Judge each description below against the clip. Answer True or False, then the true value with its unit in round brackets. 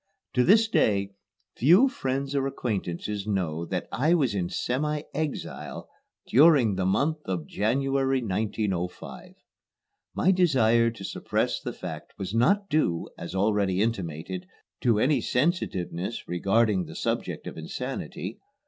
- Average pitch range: False (6.5 semitones)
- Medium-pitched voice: False (115 Hz)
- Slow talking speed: True (130 wpm)